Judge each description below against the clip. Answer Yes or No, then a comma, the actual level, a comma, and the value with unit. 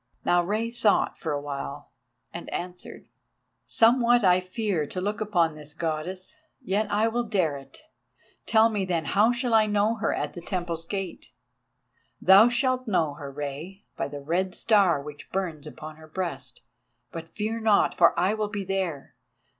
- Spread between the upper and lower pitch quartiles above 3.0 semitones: Yes, average, 5.2 semitones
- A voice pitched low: No, medium, 185 Hz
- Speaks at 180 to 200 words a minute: No, average, 165 wpm